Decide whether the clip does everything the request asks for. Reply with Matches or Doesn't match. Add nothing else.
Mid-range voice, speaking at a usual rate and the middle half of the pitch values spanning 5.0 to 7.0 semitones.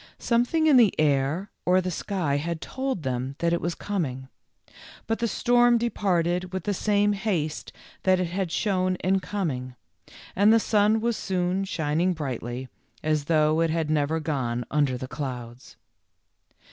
Matches